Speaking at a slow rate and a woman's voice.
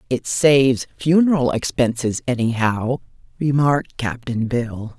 Yes: slow, 95 wpm; female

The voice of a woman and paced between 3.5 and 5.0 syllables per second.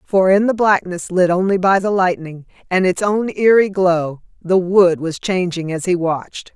Yes: female; 4.5 syllables/s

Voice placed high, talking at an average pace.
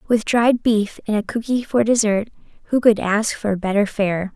Yes: high, 215 Hz; average, 195 wpm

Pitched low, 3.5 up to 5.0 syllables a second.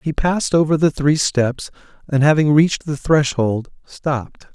No: medium, 145 Hz; 4.6 syllables/s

